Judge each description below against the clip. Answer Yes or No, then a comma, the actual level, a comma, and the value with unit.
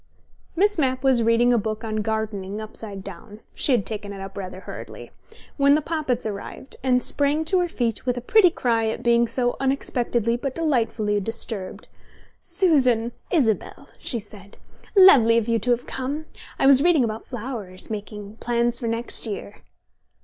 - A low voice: No, high, 235 Hz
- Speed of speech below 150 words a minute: No, average, 170 wpm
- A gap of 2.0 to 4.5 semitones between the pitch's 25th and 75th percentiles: Yes, average, 3.7 semitones